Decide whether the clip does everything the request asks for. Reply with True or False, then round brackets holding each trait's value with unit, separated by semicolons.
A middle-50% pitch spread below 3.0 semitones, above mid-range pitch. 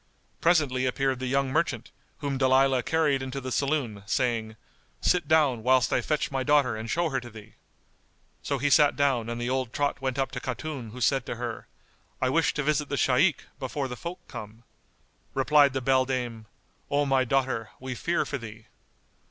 False (2.6 semitones; 130 Hz)